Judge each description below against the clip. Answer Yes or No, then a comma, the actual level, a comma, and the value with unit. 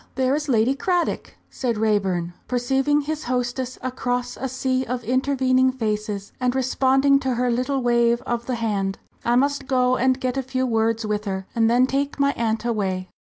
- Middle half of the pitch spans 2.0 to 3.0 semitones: Yes, narrow, 2.6 semitones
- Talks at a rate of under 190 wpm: Yes, average, 180 wpm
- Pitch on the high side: Yes, very high, 250 Hz